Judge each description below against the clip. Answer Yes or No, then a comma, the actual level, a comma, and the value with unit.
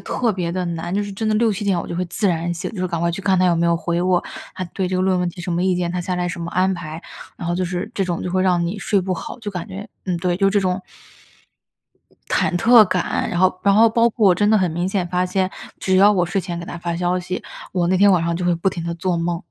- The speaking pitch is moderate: Yes, medium, 180 Hz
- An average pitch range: No, narrow, 1.9 semitones